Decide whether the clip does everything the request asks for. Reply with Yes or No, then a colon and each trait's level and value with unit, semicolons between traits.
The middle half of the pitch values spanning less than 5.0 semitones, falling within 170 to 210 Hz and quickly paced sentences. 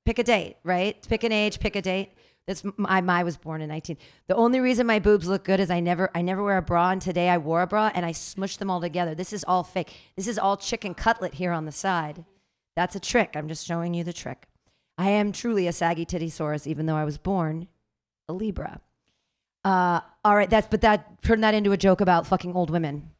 Yes: average, 3.1 semitones; medium, 185 Hz; fast, 245 wpm